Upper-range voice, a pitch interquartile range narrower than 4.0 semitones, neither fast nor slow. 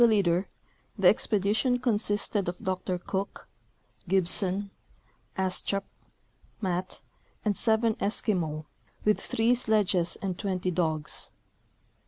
No: high, 195 Hz; average, 2.8 semitones; slow, 100 wpm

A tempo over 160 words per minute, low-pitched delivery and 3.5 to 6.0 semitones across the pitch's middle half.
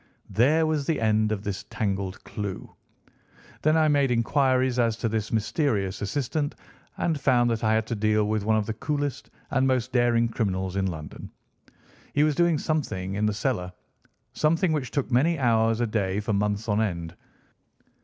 Yes: average, 175 wpm; low, 115 Hz; average, 5.0 semitones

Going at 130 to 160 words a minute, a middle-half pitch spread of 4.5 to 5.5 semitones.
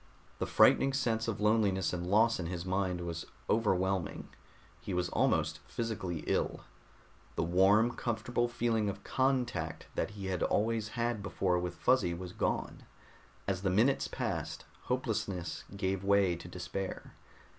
No: average, 145 wpm; average, 4.0 semitones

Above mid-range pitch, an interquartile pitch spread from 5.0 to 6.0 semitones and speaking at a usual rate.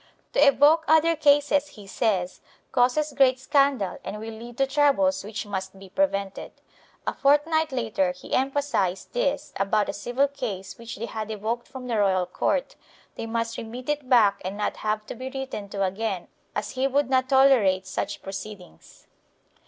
Yes: high, 235 Hz; wide, 5.6 semitones; average, 170 wpm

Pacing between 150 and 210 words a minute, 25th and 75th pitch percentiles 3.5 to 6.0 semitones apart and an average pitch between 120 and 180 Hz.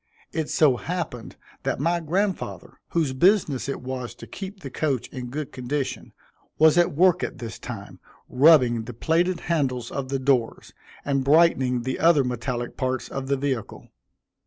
Yes: average, 160 wpm; average, 4.5 semitones; medium, 140 Hz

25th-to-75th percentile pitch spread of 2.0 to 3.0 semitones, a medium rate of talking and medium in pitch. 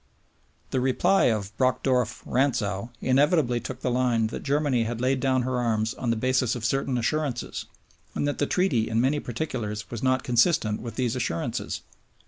No: narrow, 2.6 semitones; average, 170 wpm; low, 125 Hz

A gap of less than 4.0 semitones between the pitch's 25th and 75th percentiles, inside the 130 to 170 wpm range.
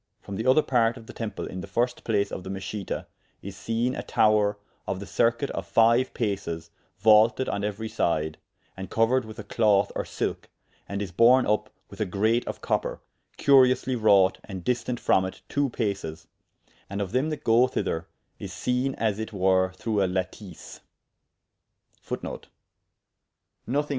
Yes: average, 3.6 semitones; average, 165 wpm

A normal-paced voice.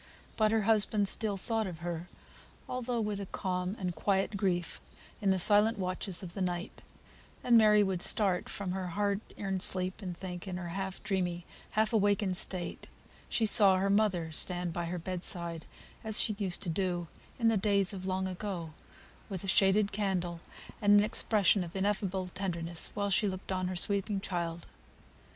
Yes: average, 180 wpm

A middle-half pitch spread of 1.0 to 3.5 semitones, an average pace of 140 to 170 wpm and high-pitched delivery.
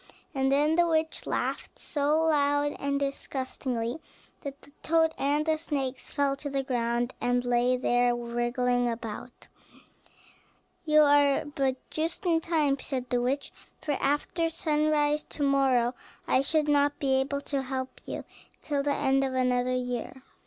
Yes: average, 2.9 semitones; average, 150 wpm; very high, 275 Hz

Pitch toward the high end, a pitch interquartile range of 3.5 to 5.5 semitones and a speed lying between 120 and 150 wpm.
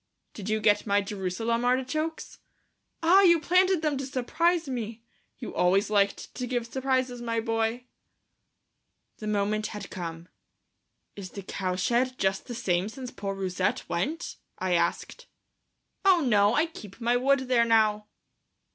Yes: high, 230 Hz; average, 4.6 semitones; average, 145 wpm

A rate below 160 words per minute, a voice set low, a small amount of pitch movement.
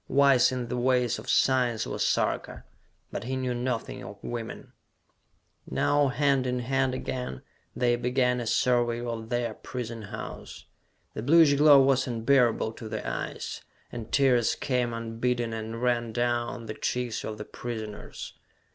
Yes: average, 150 wpm; low, 120 Hz; narrow, 1.9 semitones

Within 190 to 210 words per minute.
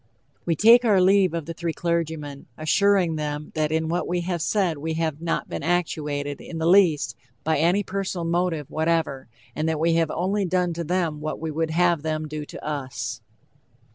Yes: average, 195 wpm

